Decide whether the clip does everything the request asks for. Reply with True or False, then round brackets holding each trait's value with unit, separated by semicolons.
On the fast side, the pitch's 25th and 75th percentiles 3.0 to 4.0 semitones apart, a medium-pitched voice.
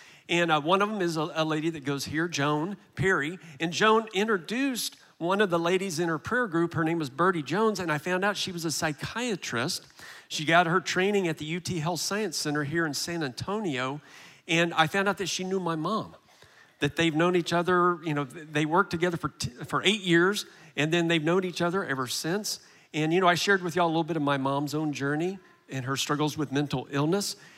True (230 wpm; 3.4 semitones; 170 Hz)